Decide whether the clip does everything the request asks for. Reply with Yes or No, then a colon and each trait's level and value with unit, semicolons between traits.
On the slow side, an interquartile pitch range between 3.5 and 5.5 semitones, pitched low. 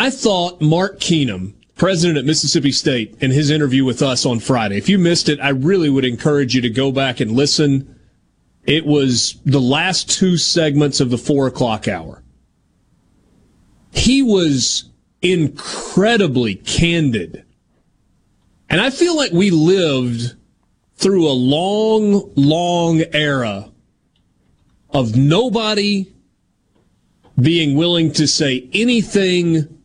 No: slow, 125 wpm; average, 5.1 semitones; medium, 150 Hz